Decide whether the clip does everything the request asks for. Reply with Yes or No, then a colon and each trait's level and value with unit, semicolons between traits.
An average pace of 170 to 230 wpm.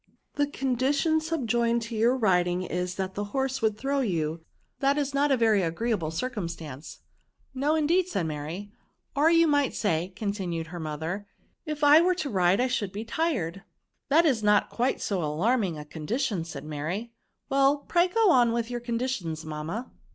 Yes: average, 180 wpm